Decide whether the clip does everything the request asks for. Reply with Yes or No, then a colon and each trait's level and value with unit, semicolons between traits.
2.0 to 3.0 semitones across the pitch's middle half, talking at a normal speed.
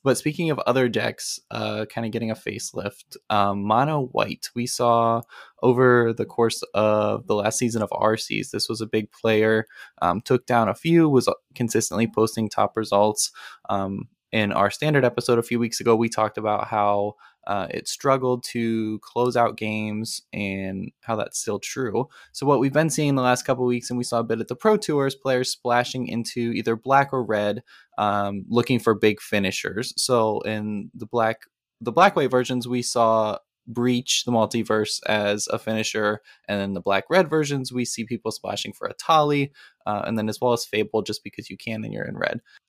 Yes: narrow, 2.6 semitones; average, 195 wpm